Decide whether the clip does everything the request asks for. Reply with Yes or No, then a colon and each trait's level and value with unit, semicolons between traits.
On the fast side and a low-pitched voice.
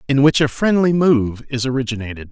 No: average, 180 wpm; low, 130 Hz